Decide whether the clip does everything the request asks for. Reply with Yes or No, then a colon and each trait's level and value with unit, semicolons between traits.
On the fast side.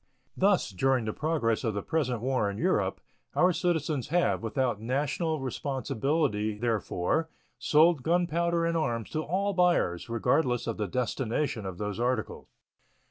No: average, 140 wpm